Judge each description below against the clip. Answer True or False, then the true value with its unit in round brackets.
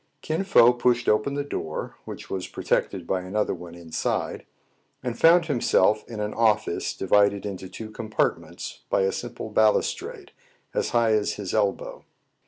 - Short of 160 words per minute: False (165 wpm)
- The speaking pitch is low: True (105 Hz)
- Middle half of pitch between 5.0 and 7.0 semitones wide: False (3.7 semitones)